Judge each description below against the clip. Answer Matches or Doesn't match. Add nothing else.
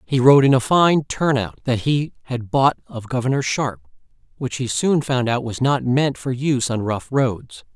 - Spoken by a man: Matches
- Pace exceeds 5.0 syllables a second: Doesn't match